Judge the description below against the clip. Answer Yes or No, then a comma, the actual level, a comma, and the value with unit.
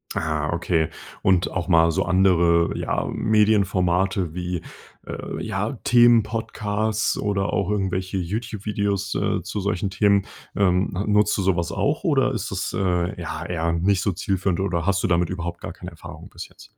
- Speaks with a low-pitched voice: Yes, very low, 95 Hz